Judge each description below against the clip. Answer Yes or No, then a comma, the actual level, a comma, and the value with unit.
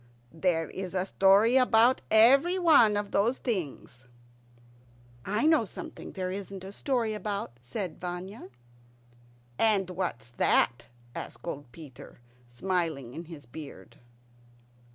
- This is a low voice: No, high, 190 Hz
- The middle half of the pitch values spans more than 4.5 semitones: Yes, wide, 5.5 semitones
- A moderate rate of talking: No, slow, 115 wpm